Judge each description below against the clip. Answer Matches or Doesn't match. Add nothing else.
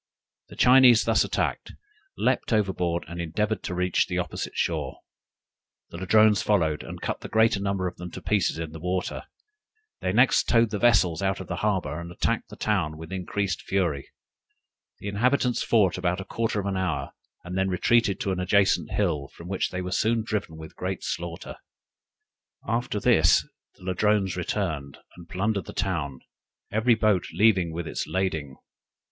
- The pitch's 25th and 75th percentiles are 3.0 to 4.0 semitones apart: Matches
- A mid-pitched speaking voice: Doesn't match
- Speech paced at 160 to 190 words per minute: Matches